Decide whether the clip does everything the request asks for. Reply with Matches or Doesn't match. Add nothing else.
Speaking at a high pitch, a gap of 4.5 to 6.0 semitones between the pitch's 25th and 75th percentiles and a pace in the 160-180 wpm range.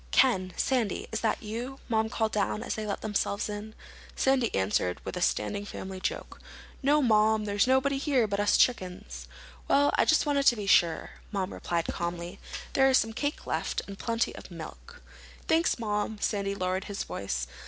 Matches